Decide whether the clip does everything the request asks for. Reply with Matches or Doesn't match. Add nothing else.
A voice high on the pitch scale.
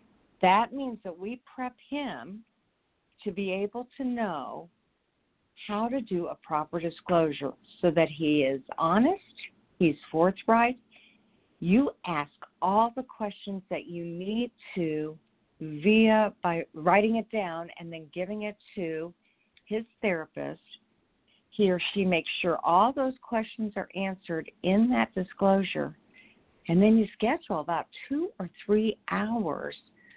Matches